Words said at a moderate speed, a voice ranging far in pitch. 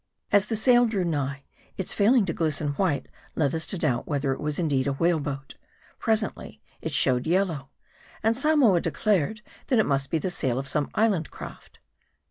Yes: average, 185 wpm; wide, 6.9 semitones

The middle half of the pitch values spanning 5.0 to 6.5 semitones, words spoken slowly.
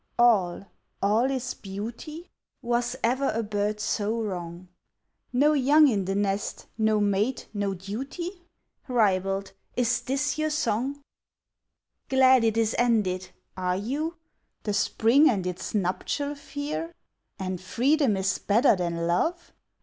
Yes: wide, 5.6 semitones; slow, 125 wpm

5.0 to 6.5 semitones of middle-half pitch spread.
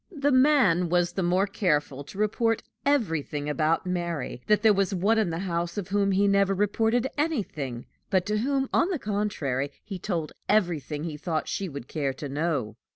Yes: average, 5.3 semitones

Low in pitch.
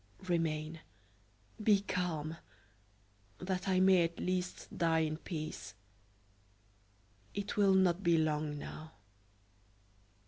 No: medium, 170 Hz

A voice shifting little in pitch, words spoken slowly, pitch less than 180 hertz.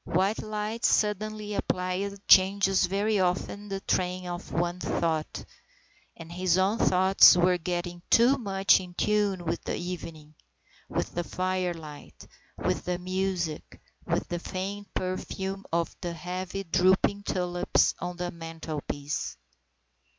No: narrow, 2.0 semitones; slow, 130 wpm; medium, 185 Hz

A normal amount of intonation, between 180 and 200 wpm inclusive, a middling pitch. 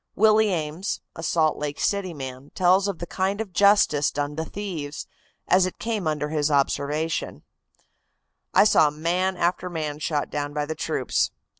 No: average, 4.2 semitones; average, 165 wpm; medium, 160 Hz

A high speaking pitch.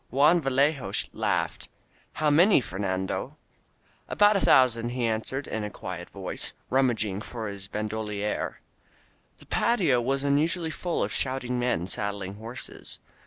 No: low, 125 Hz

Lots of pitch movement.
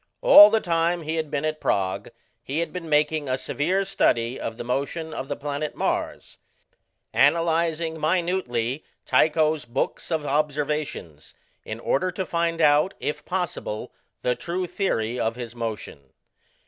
No: average, 4.7 semitones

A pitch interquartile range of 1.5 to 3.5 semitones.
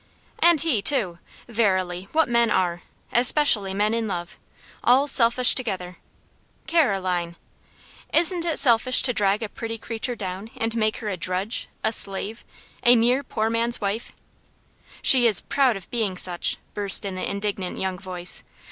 No: average, 4.2 semitones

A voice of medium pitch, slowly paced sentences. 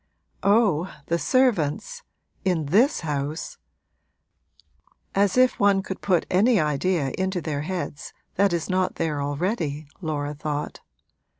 Yes: medium, 175 Hz; slow, 120 wpm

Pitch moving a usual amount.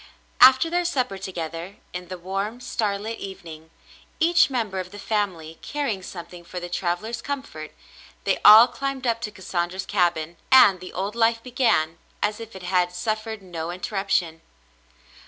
Yes: average, 4.5 semitones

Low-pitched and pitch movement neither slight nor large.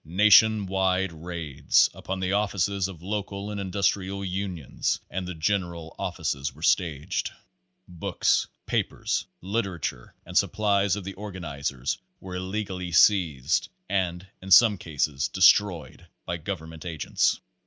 Yes: very low, 95 Hz; average, 3.3 semitones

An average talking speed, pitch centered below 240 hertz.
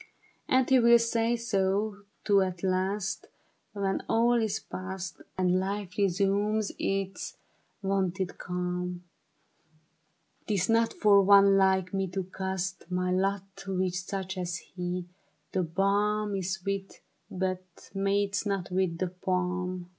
No: slow, 130 wpm; high, 190 Hz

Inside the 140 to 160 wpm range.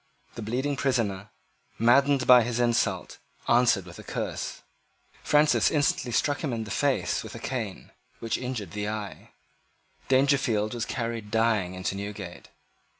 Yes: average, 145 wpm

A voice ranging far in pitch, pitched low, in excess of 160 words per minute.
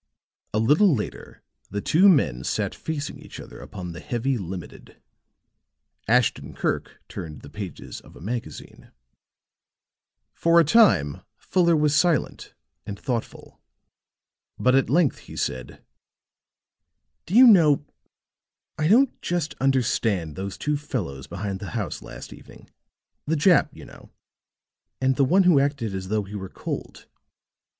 No: wide, 8.2 semitones; low, 130 Hz; average, 140 wpm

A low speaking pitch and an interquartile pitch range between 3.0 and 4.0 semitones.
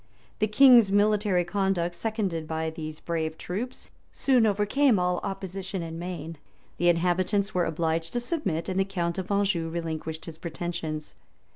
No: medium, 180 Hz; average, 3.6 semitones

